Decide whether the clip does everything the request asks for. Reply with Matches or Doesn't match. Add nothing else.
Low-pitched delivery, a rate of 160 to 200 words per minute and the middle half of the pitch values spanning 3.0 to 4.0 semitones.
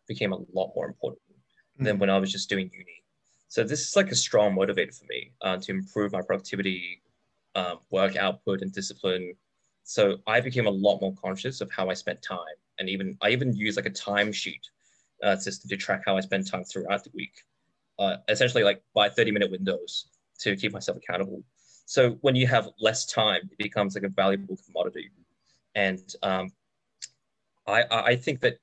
Matches